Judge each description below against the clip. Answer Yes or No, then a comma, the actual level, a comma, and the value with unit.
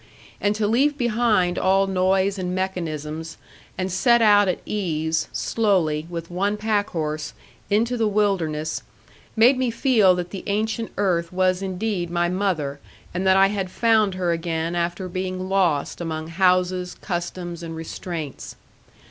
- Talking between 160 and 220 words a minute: No, average, 145 wpm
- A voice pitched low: No, medium, 185 Hz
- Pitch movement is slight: No, average, 3.3 semitones